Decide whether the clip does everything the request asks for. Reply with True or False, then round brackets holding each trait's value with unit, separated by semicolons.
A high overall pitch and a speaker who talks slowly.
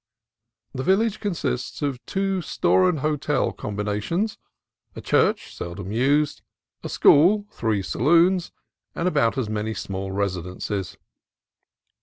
False (135 Hz; 120 wpm)